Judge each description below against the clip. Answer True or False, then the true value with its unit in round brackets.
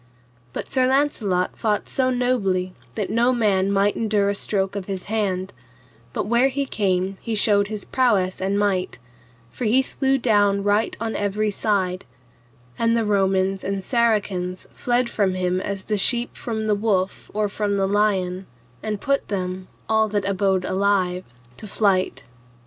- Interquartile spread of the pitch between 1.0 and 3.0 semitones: True (2.7 semitones)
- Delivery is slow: False (160 wpm)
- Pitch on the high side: True (205 Hz)